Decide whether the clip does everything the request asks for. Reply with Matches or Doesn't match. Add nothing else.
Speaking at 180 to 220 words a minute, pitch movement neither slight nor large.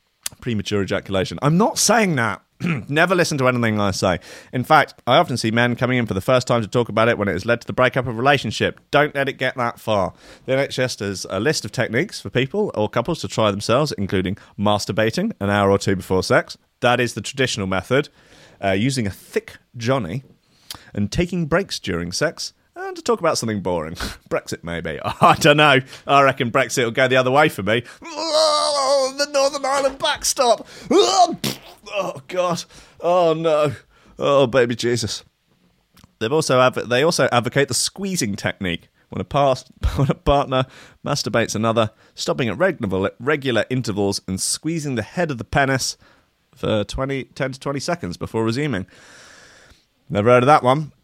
Doesn't match